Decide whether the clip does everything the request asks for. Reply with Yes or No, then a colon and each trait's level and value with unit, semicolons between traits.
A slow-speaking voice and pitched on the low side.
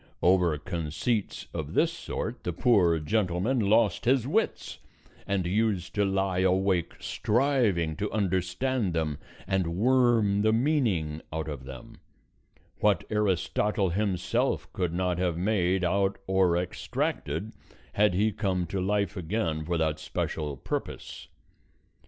Yes: slow, 130 wpm; very low, 95 Hz